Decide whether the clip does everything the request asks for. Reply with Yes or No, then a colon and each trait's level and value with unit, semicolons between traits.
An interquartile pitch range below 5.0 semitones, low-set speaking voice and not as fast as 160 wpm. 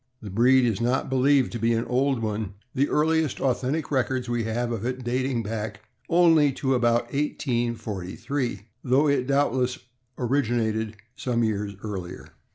Yes: average, 3.1 semitones; low, 120 Hz; average, 150 wpm